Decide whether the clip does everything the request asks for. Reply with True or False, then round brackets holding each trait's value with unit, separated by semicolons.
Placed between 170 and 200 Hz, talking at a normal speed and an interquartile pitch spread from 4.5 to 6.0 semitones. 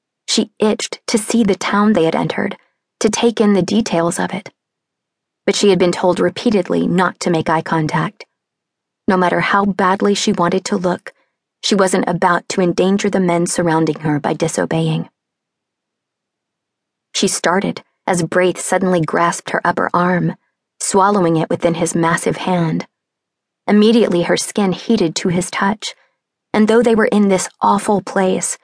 False (185 Hz; 160 wpm; 3.1 semitones)